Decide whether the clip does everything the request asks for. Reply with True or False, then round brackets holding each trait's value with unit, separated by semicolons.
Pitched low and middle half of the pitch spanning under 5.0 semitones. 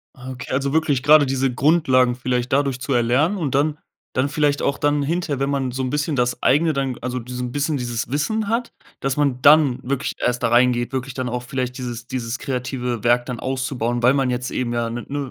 True (130 Hz; 2.6 semitones)